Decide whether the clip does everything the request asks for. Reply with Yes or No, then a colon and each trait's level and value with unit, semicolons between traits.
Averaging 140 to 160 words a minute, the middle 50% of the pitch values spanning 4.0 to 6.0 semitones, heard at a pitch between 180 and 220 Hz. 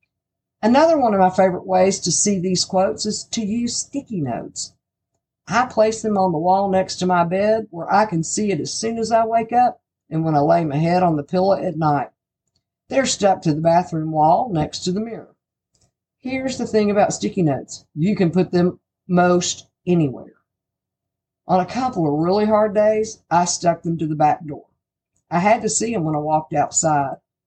No: average, 200 wpm; average, 4.4 semitones; medium, 185 Hz